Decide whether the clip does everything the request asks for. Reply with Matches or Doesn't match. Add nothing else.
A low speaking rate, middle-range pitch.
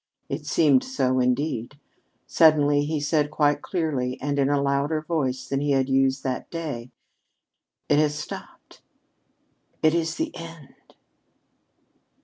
Matches